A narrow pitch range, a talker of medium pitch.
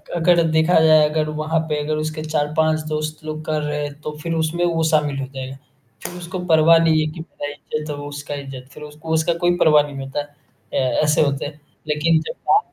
Yes: narrow, 1.5 semitones; medium, 155 Hz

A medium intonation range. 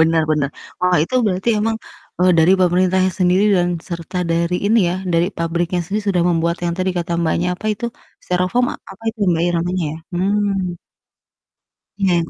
No: narrow, 1.9 semitones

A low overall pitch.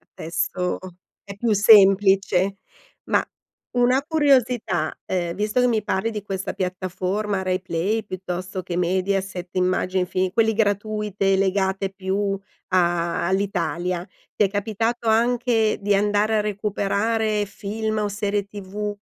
No: high, 200 Hz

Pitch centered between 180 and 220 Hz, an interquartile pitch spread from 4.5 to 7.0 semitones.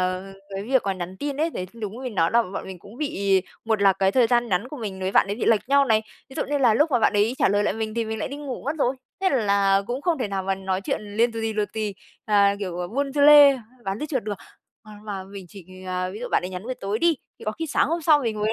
Yes: high, 215 Hz; average, 5.1 semitones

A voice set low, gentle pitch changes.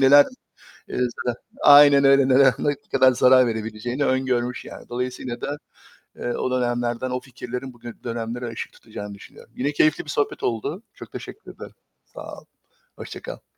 Yes: low, 125 Hz; narrow, 2.3 semitones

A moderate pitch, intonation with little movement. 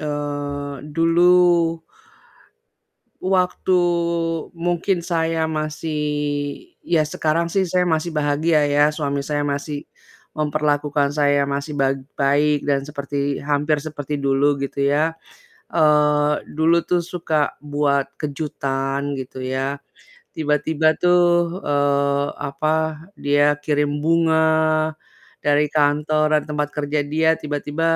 Yes: medium, 150 Hz; narrow, 1.8 semitones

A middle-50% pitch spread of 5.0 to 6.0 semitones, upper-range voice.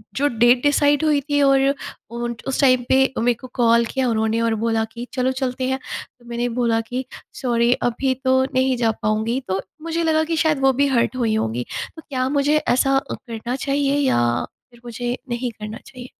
No: narrow, 2.6 semitones; very high, 255 Hz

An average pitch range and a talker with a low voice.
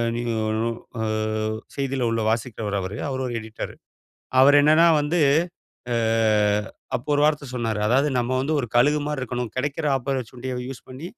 Yes: average, 3.4 semitones; low, 130 Hz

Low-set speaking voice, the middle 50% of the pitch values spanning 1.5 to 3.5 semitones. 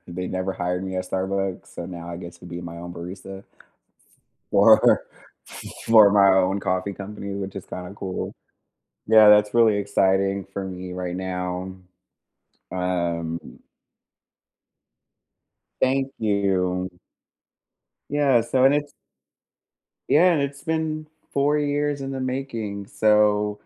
No: low, 100 Hz; average, 4.2 semitones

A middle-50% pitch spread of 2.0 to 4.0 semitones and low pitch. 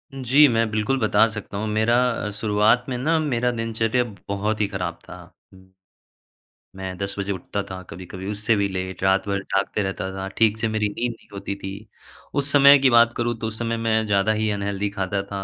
Yes: average, 2.7 semitones; low, 105 Hz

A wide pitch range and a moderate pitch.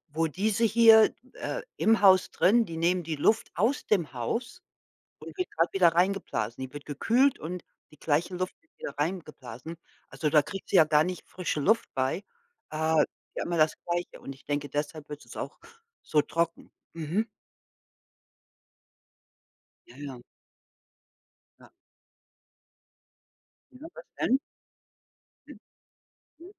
Yes: wide, 5.7 semitones; medium, 170 Hz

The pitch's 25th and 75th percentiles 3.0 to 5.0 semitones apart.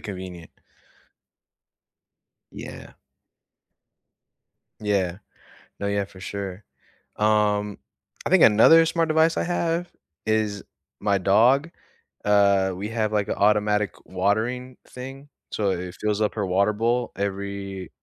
No: narrow, 2.6 semitones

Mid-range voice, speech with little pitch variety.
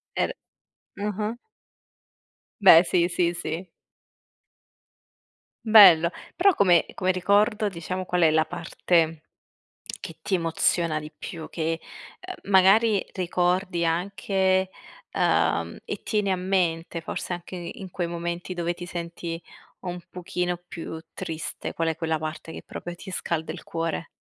Yes: medium, 175 Hz; narrow, 2.3 semitones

